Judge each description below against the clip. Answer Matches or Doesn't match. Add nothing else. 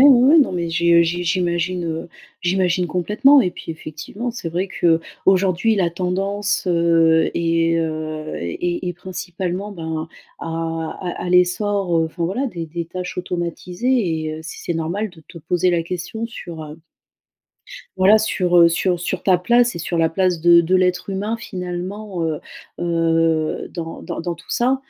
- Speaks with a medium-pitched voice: Matches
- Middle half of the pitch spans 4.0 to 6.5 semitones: Doesn't match